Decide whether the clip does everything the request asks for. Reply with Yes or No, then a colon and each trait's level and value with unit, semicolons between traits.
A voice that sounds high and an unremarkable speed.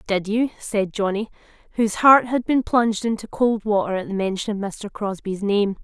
Yes: high, 210 Hz; average, 195 wpm